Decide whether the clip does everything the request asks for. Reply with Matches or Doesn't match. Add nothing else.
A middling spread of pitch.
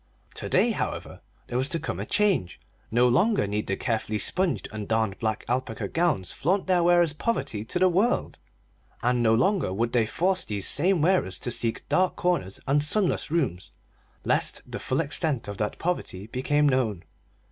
Doesn't match